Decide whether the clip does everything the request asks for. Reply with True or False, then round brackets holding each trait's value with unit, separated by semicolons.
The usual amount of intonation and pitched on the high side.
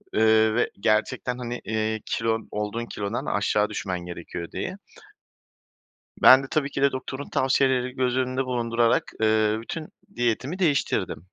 False (3.2 semitones; 115 Hz)